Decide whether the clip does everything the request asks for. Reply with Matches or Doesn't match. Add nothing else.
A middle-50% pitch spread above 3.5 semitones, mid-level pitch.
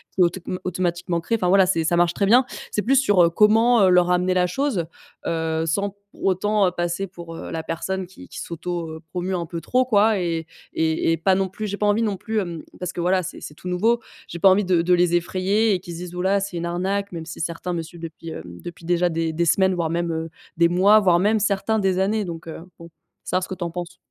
Doesn't match